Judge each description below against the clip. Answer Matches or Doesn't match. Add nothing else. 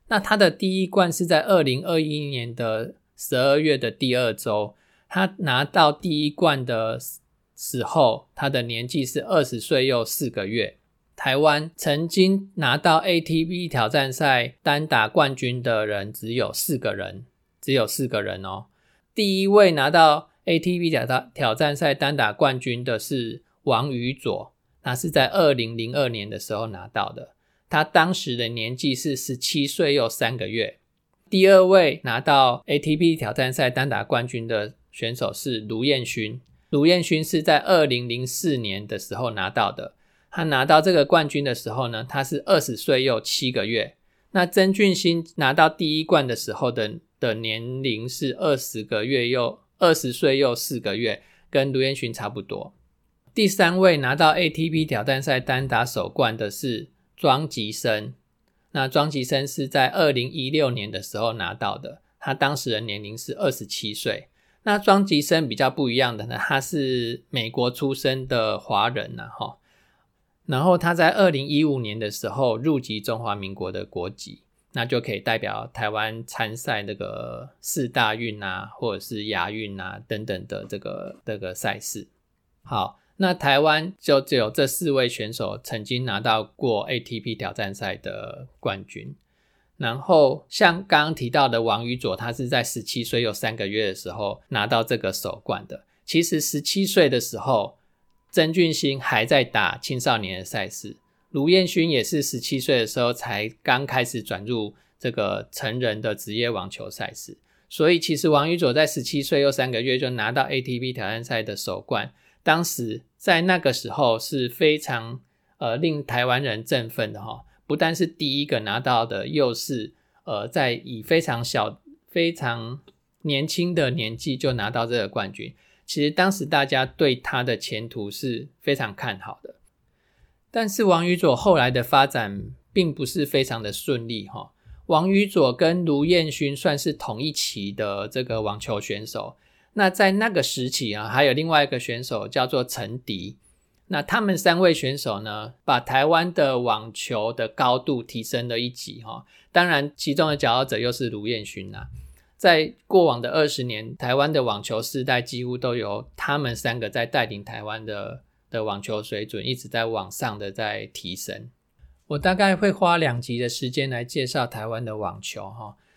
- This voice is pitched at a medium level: Doesn't match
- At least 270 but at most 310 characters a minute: Doesn't match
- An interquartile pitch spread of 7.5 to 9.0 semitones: Doesn't match